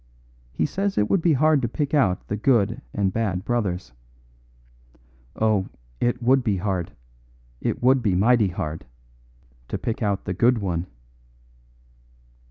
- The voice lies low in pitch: Yes, low, 110 Hz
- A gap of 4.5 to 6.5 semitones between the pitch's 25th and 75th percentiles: Yes, average, 5.0 semitones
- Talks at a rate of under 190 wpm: Yes, average, 145 wpm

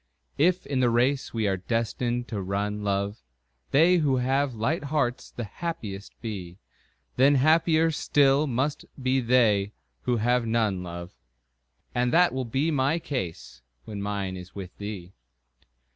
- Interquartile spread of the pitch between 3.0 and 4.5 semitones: No, wide, 5.6 semitones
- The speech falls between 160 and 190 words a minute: No, average, 145 wpm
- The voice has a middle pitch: No, low, 120 Hz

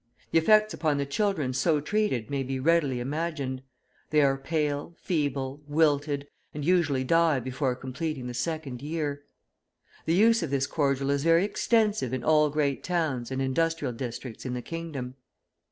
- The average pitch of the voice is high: No, medium, 145 Hz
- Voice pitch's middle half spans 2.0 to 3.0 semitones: No, average, 3.8 semitones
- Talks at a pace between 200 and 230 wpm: No, average, 160 wpm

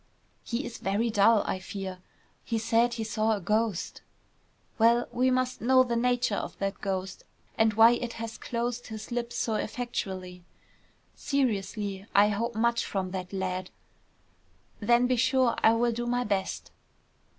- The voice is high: Yes, high, 225 Hz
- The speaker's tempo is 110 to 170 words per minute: Yes, average, 155 wpm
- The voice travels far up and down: No, average, 3.3 semitones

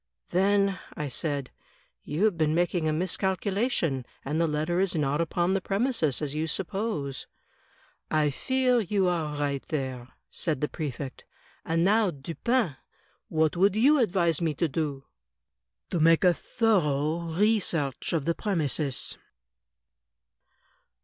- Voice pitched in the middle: Yes, medium, 165 Hz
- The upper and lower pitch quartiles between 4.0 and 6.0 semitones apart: Yes, average, 4.6 semitones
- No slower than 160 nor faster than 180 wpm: No, average, 140 wpm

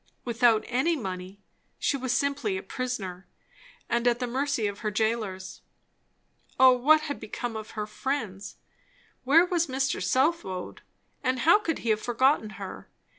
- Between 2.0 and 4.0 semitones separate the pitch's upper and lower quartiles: No, average, 4.6 semitones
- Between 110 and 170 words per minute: Yes, average, 150 wpm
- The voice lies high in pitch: Yes, high, 245 Hz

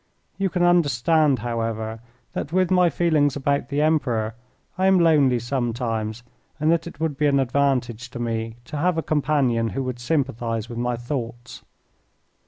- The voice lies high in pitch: No, low, 135 Hz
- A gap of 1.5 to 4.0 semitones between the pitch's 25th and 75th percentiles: No, average, 4.6 semitones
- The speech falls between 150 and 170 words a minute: Yes, average, 165 wpm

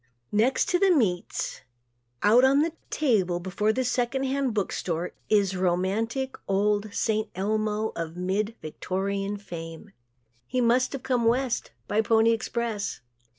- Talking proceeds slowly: No, average, 145 wpm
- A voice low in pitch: No, high, 215 Hz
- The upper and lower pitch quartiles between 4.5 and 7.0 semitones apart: No, average, 4.1 semitones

